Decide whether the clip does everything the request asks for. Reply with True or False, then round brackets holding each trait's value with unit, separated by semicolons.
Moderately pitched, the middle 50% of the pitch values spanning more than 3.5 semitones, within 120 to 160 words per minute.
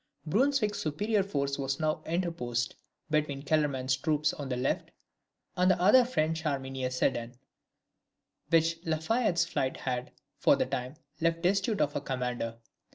True (155 Hz; 4.8 semitones; 150 wpm)